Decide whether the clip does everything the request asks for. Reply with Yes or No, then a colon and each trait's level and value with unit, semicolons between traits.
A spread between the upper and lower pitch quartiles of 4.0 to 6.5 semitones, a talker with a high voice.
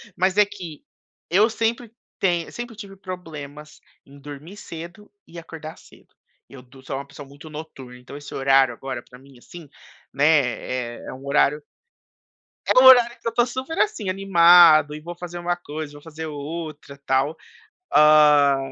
No: average, 4.7 semitones; medium, 155 Hz